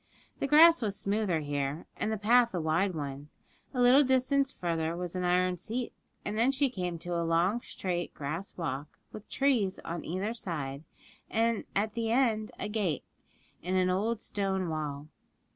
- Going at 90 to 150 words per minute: No, average, 175 wpm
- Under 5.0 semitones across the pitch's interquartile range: No, wide, 5.6 semitones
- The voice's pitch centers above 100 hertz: Yes, high, 190 Hz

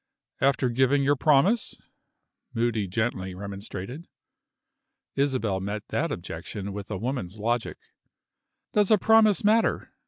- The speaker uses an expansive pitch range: Yes, wide, 6.0 semitones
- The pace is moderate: No, slow, 115 wpm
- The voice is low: Yes, low, 120 Hz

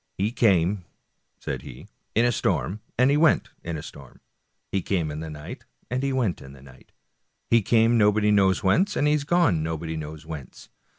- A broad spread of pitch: Yes, wide, 7.1 semitones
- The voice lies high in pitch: No, low, 100 Hz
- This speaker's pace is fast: Yes, fast, 210 wpm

